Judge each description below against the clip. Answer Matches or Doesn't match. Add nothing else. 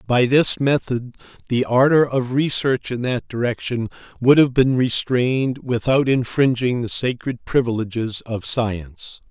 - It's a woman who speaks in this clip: Doesn't match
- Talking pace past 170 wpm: Doesn't match